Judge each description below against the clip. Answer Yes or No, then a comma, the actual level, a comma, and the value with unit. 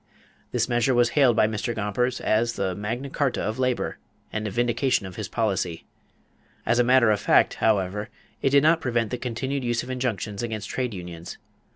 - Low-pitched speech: Yes, low, 115 Hz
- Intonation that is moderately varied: Yes, average, 3.2 semitones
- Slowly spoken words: No, average, 190 wpm